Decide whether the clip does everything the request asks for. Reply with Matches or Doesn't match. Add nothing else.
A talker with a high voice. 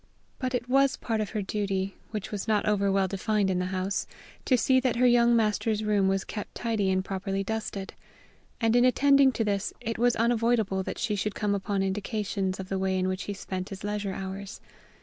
Matches